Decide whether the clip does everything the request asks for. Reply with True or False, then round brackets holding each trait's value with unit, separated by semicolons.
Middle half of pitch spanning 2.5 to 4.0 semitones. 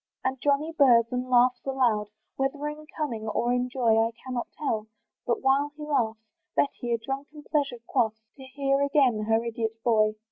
True (3.6 semitones)